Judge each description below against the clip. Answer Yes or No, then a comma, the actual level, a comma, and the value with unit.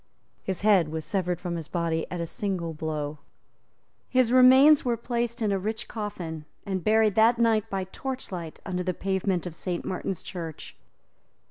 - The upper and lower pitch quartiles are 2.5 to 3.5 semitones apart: No, average, 4.7 semitones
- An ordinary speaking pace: Yes, average, 165 wpm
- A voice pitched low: No, high, 190 Hz